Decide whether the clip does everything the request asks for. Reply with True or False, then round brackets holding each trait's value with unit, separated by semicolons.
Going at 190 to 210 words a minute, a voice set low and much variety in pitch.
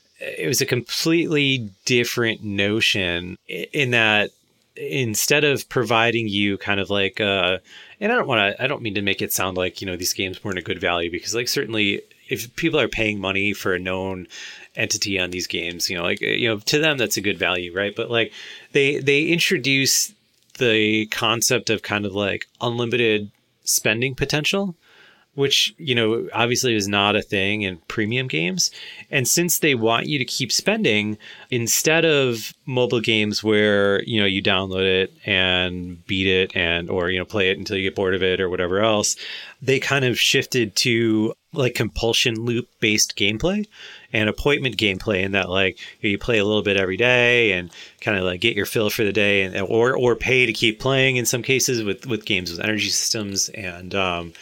False (195 wpm; 110 Hz; 4.3 semitones)